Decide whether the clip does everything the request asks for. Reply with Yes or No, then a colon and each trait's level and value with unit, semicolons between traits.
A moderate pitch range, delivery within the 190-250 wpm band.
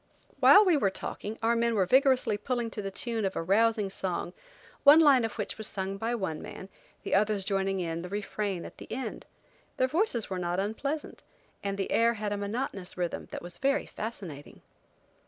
Yes: average, 3.6 semitones; average, 195 wpm